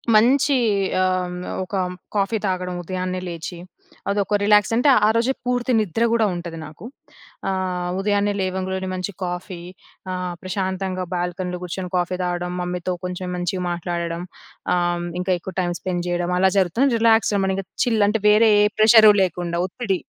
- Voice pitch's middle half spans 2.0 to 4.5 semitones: Yes, narrow, 2.6 semitones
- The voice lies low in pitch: No, medium, 185 Hz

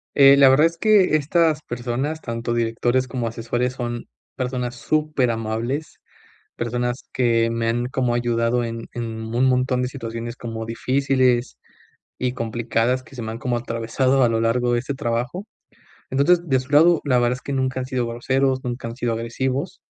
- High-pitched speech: No, low, 125 Hz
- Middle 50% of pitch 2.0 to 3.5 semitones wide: Yes, narrow, 2.4 semitones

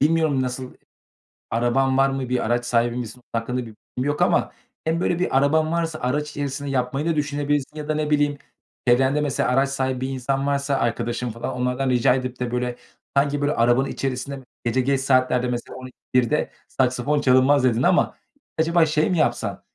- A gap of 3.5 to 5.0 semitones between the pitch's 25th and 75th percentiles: No, narrow, 2.6 semitones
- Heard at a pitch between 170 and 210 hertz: No, low, 135 Hz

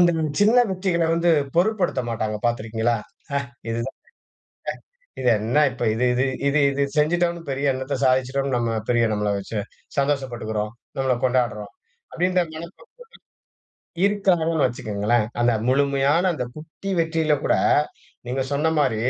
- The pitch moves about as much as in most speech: No, wide, 5.7 semitones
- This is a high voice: No, low, 135 Hz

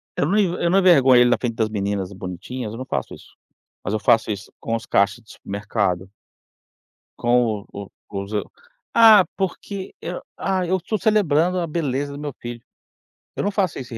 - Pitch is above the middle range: No, low, 125 Hz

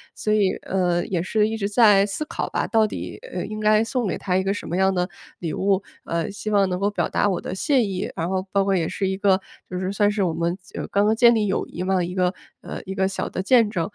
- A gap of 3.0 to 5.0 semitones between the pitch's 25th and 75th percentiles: No, narrow, 2.4 semitones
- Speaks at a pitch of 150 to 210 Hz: Yes, high, 195 Hz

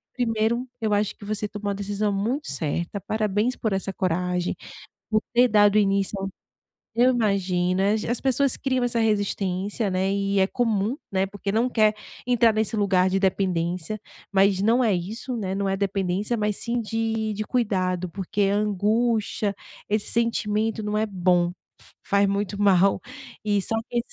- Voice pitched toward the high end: Yes, high, 205 Hz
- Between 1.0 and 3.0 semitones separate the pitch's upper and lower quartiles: Yes, narrow, 2.5 semitones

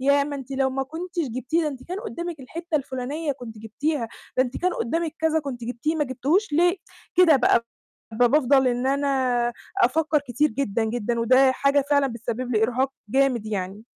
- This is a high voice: Yes, very high, 270 Hz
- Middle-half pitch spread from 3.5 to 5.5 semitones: Yes, average, 3.8 semitones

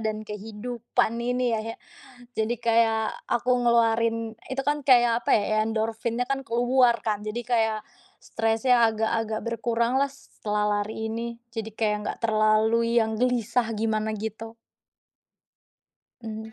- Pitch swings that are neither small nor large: No, narrow, 1.6 semitones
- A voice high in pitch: Yes, high, 225 Hz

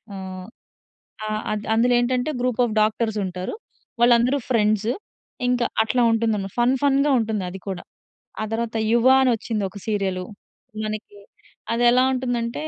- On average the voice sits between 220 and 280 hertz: Yes, high, 230 Hz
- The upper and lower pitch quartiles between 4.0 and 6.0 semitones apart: No, average, 2.8 semitones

